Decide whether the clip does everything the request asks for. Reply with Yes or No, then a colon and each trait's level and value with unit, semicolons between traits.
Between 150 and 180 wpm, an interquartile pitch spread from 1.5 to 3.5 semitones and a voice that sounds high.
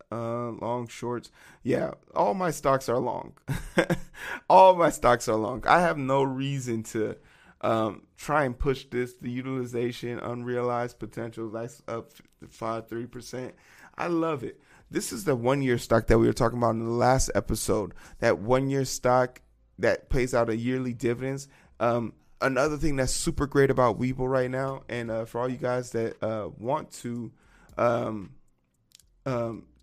No: average, 165 wpm; narrow, 2.4 semitones; low, 120 Hz